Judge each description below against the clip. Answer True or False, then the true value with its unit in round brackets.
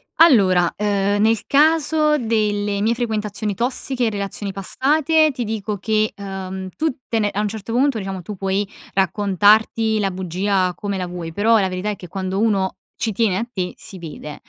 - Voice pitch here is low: False (205 Hz)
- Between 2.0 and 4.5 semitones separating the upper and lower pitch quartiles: True (2.9 semitones)